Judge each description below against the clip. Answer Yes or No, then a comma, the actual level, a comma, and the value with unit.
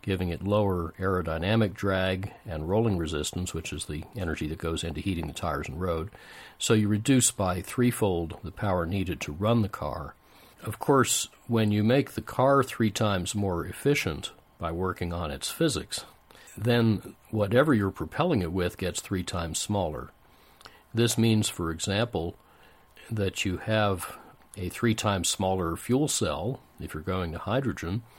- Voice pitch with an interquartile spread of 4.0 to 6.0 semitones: Yes, average, 4.3 semitones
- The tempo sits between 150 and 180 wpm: Yes, average, 160 wpm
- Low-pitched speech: Yes, very low, 95 Hz